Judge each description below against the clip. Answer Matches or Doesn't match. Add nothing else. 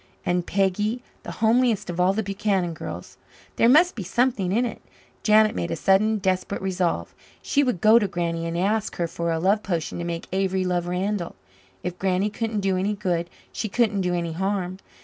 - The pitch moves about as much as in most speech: Matches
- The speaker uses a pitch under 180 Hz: Doesn't match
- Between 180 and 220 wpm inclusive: Matches